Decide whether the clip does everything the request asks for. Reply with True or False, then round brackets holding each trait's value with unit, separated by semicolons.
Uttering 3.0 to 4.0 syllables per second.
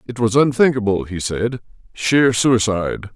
False (4.7 syllables/s)